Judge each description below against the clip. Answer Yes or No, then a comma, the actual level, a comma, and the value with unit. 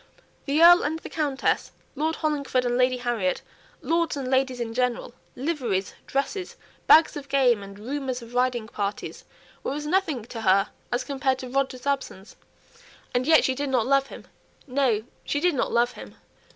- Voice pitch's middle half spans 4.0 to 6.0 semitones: No, average, 3.1 semitones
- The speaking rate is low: No, average, 170 wpm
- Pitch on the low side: No, very high, 260 Hz